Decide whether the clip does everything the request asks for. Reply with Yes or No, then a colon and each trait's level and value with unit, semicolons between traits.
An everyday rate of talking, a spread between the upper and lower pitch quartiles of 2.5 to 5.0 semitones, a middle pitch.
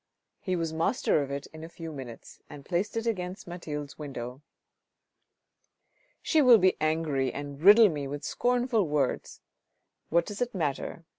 No: average, 160 wpm; wide, 5.5 semitones; medium, 160 Hz